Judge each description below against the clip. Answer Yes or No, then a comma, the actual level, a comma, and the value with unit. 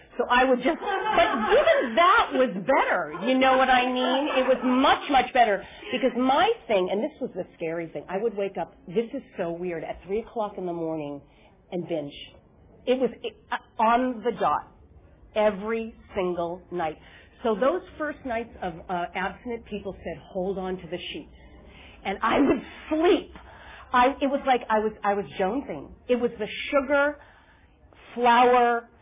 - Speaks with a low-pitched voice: No, high, 230 Hz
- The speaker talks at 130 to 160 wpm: No, average, 175 wpm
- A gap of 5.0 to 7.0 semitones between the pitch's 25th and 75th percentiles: Yes, wide, 5.4 semitones